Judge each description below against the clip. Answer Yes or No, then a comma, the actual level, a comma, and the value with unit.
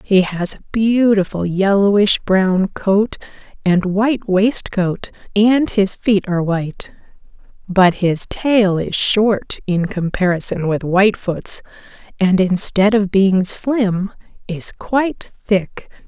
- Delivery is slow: Yes, slow, 120 wpm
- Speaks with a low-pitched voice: No, high, 195 Hz